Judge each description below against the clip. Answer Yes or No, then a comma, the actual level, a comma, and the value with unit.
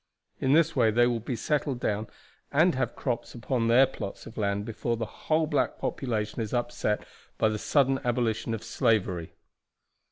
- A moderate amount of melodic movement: Yes, average, 3.4 semitones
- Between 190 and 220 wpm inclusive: No, average, 170 wpm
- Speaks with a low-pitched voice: Yes, low, 120 Hz